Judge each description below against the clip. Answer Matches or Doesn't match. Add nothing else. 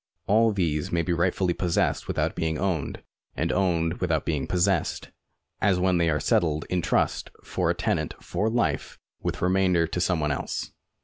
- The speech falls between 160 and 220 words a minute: Matches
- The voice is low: Matches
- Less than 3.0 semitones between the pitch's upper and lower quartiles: Matches